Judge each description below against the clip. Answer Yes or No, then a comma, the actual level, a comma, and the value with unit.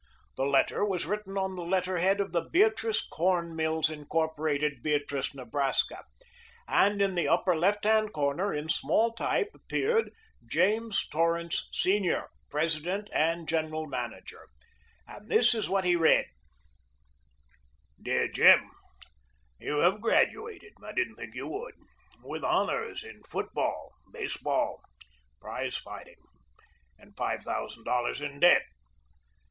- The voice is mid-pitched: Yes, medium, 175 Hz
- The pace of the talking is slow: Yes, slow, 125 wpm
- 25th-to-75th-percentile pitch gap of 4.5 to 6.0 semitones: Yes, average, 5.1 semitones